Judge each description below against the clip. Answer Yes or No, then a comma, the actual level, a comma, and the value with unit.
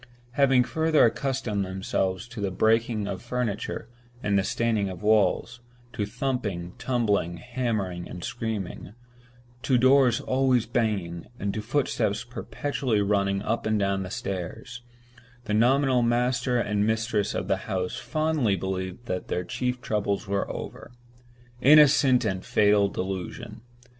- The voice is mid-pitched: No, low, 110 Hz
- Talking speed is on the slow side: Yes, slow, 130 wpm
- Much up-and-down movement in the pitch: No, average, 4.0 semitones